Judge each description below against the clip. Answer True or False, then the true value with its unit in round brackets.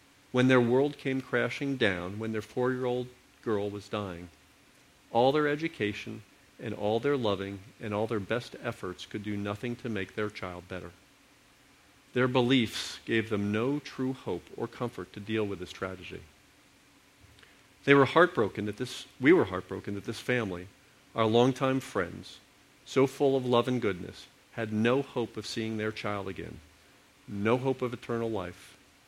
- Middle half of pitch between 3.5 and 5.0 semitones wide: True (4.3 semitones)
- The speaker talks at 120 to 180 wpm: True (165 wpm)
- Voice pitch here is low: True (115 Hz)